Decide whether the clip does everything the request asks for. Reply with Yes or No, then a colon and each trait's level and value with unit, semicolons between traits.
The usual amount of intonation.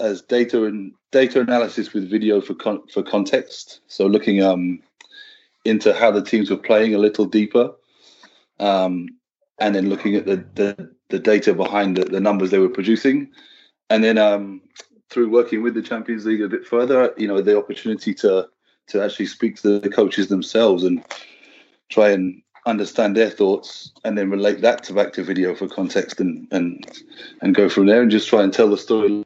Yes: average, 3.3 semitones